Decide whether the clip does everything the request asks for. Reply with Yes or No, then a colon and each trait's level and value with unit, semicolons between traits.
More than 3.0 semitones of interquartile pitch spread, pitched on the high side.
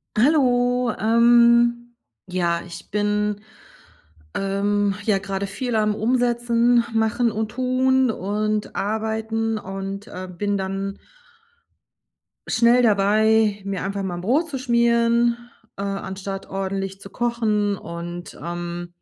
Yes: average, 3.4 semitones; high, 215 Hz